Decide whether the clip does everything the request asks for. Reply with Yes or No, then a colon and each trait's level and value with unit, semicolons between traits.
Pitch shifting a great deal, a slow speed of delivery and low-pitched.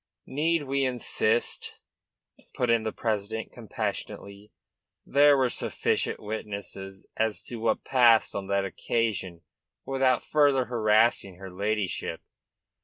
No: average, 4.1 semitones; slow, 110 wpm; low, 110 Hz